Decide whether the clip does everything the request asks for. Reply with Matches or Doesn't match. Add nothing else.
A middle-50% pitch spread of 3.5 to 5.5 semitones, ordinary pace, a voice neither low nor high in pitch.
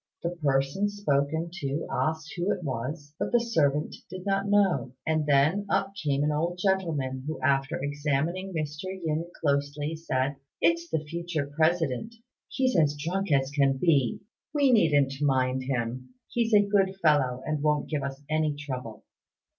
Matches